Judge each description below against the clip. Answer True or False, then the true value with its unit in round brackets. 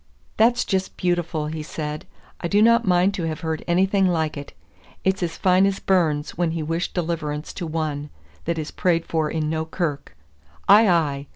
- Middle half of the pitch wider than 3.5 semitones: False (3.1 semitones)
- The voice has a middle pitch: True (165 Hz)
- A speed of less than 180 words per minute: False (185 wpm)